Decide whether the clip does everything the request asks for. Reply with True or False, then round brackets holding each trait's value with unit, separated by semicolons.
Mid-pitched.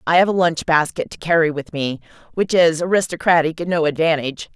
True (165 Hz)